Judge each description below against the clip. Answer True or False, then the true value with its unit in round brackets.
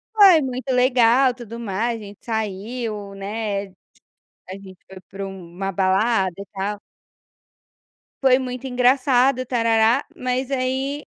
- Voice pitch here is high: True (230 Hz)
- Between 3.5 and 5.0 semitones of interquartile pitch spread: True (4.4 semitones)